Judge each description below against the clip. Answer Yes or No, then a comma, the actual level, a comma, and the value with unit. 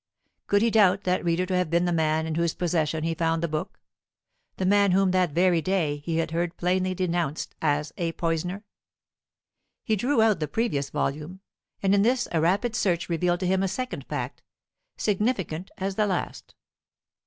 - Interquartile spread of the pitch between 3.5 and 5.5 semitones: No, average, 2.9 semitones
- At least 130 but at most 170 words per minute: No, average, 185 wpm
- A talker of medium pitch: Yes, medium, 180 Hz